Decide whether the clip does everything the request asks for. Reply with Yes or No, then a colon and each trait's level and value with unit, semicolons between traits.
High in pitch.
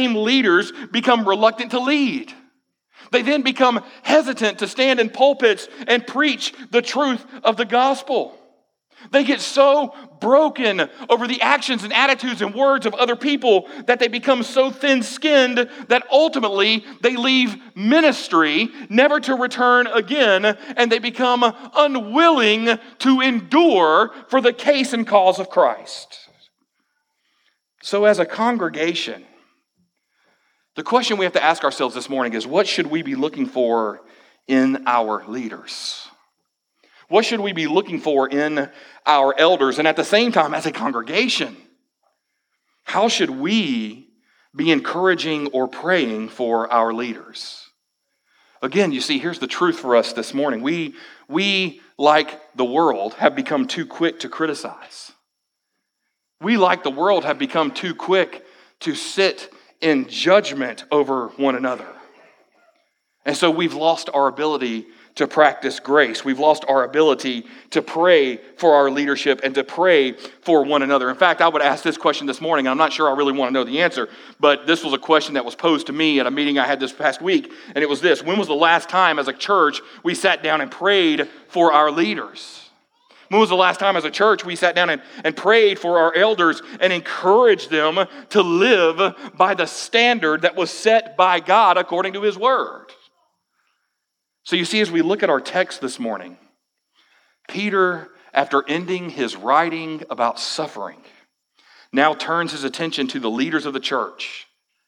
Yes: high, 195 Hz